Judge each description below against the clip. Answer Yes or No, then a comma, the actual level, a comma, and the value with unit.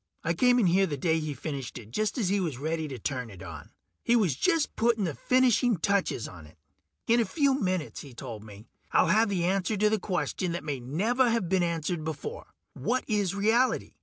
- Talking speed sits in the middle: No, fast, 220 wpm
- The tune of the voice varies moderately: No, wide, 7.5 semitones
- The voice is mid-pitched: Yes, medium, 180 Hz